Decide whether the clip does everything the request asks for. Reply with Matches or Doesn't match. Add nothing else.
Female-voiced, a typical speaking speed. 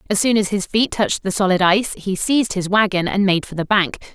Doesn't match